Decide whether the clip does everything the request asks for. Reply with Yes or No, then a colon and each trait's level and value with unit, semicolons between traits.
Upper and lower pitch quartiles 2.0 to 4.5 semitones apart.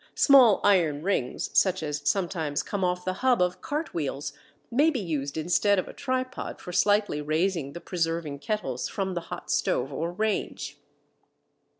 No: average, 5.0 semitones